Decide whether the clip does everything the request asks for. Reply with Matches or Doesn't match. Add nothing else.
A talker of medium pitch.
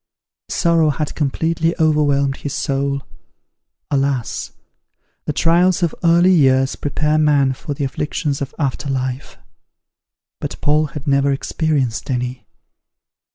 Matches